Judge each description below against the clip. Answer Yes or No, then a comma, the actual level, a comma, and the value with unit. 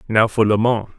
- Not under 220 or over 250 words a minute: Yes, fast, 245 wpm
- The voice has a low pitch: Yes, low, 110 Hz